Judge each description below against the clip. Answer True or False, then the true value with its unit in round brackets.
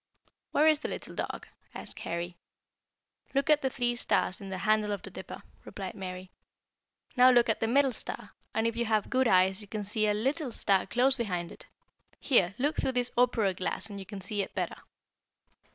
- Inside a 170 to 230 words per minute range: True (200 wpm)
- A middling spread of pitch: True (4.5 semitones)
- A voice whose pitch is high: True (215 Hz)